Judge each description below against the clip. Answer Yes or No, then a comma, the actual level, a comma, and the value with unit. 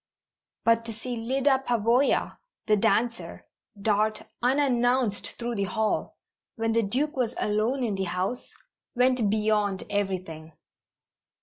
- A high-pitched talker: Yes, high, 225 Hz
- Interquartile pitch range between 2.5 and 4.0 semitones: Yes, average, 3.3 semitones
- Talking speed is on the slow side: Yes, slow, 120 wpm